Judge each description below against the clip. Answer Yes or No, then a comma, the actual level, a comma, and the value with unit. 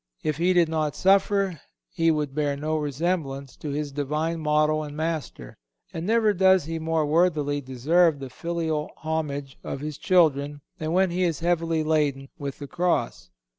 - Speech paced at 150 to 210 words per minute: Yes, average, 170 wpm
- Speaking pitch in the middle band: Yes, medium, 155 Hz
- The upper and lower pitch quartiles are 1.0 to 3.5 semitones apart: Yes, average, 2.8 semitones